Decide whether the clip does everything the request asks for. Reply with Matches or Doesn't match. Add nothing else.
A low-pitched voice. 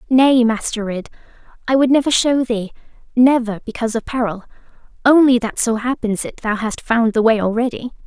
Doesn't match